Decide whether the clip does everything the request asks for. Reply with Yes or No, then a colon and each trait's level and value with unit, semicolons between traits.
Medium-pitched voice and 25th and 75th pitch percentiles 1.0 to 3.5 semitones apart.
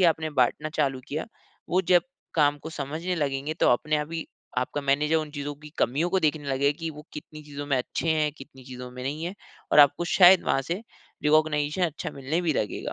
Yes: medium, 150 Hz; narrow, 2.4 semitones